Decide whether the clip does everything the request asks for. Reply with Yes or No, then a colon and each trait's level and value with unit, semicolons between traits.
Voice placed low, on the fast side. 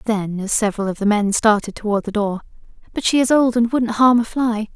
No: high, 220 Hz; fast, 240 wpm